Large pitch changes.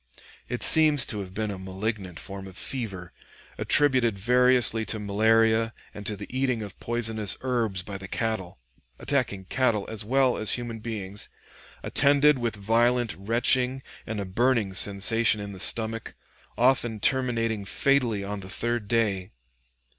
No: average, 3.4 semitones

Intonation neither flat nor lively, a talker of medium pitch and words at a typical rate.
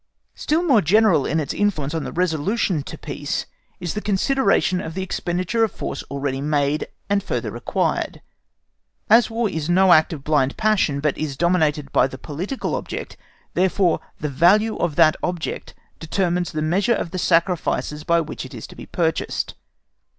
Yes: average, 4.6 semitones; medium, 170 Hz; average, 170 wpm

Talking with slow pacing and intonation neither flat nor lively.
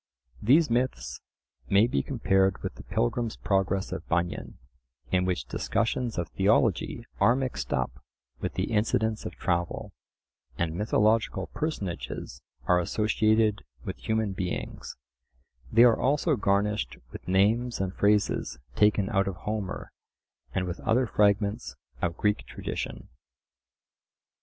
Yes: slow, 125 wpm; average, 3.3 semitones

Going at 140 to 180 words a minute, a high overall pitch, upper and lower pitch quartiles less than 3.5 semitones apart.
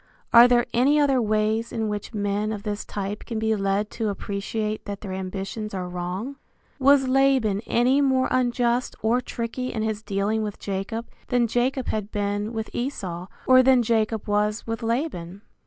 Yes: average, 170 wpm; high, 220 Hz; average, 3.1 semitones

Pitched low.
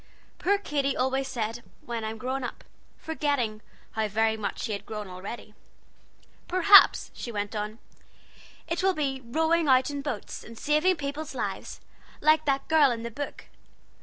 No: very high, 265 Hz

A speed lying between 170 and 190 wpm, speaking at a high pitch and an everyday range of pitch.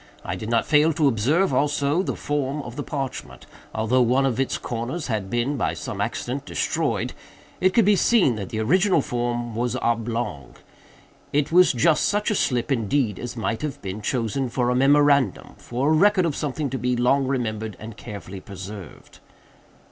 No: average, 180 wpm; low, 130 Hz; average, 4.3 semitones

